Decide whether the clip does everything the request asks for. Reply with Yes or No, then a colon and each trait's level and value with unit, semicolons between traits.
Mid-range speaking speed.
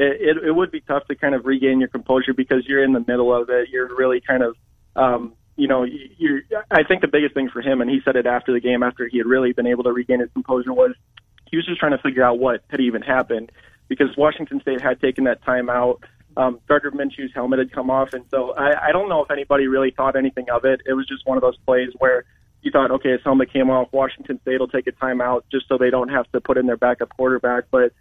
No: fast, 265 wpm